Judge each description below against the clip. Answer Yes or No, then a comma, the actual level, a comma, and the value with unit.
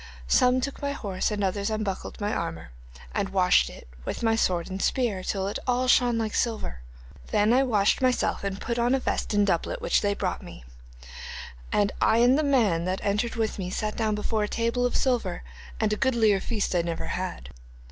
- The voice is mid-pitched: No, high, 215 Hz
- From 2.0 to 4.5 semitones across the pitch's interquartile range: Yes, average, 3.9 semitones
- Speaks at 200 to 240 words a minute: Yes, fast, 205 wpm